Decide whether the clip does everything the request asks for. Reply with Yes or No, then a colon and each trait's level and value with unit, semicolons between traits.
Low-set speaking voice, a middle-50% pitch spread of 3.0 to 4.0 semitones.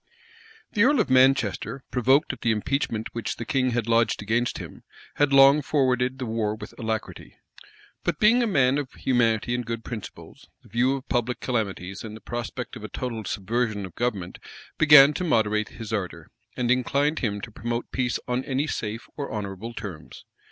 Yes: low, 120 Hz; average, 3.4 semitones